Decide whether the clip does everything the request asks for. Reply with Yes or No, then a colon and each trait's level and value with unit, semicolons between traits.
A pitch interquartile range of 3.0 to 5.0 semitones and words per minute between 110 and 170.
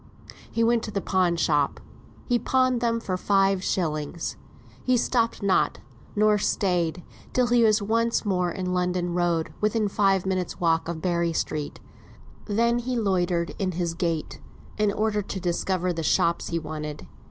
Yes: average, 4.0 semitones; average, 160 wpm